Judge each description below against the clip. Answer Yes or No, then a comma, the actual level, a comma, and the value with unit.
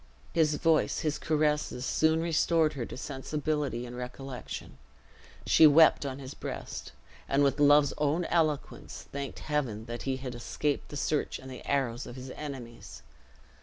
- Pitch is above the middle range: No, medium, 140 Hz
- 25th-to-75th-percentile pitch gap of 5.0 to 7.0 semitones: No, average, 2.8 semitones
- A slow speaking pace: No, average, 155 wpm